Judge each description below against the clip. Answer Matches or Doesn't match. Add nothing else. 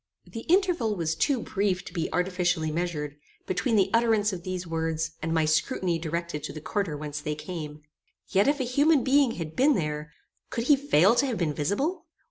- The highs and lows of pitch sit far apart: Matches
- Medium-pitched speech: Matches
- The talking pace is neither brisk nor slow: Matches